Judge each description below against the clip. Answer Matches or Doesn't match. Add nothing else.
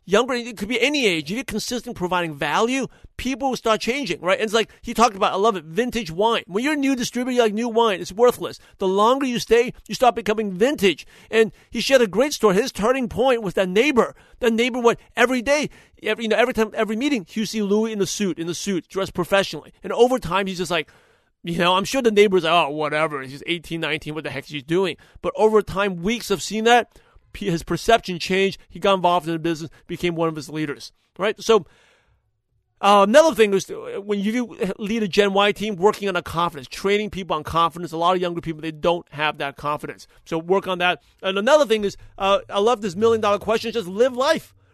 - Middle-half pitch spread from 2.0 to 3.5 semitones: Doesn't match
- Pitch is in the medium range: Doesn't match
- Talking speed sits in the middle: Doesn't match